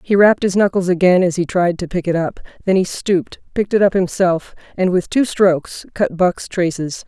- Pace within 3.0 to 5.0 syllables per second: No, 5.4 syllables/s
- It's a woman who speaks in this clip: Yes, female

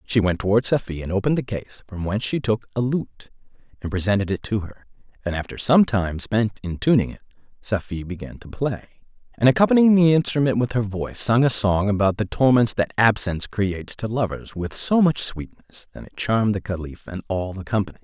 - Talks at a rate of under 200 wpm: No, fast, 205 wpm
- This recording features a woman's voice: No, male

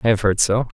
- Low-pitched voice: Yes, low, 105 Hz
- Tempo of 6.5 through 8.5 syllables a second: Yes, 6.6 syllables/s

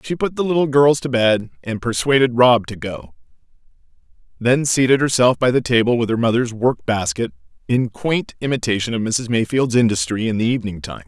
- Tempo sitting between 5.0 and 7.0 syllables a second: Yes, 5.4 syllables/s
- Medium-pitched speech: No, low, 120 Hz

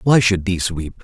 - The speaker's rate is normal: No, fast, 235 wpm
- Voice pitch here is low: Yes, very low, 95 Hz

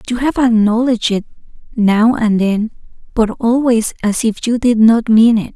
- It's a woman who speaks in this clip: Yes, female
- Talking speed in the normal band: Yes, average, 175 wpm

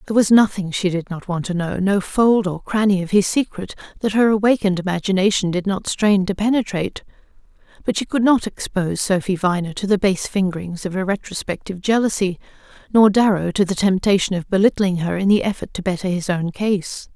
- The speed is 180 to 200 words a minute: Yes, average, 195 wpm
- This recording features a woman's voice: Yes, female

